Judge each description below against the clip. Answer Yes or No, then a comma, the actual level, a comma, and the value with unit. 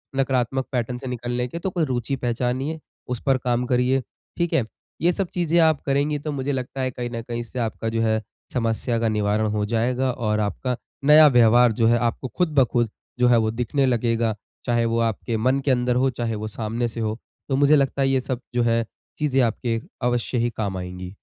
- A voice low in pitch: Yes, low, 125 Hz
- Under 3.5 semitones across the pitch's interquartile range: Yes, narrow, 2.6 semitones